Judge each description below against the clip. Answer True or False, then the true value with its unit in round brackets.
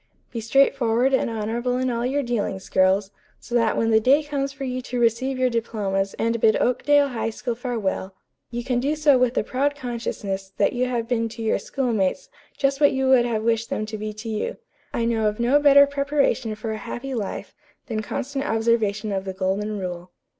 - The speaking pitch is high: True (235 Hz)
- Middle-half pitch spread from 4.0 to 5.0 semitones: False (3.3 semitones)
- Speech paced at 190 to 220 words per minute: True (205 wpm)